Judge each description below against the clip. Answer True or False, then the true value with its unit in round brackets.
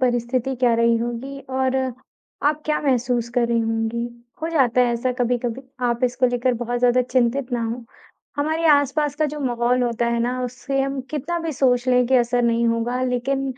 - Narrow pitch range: True (2.1 semitones)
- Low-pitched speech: False (250 Hz)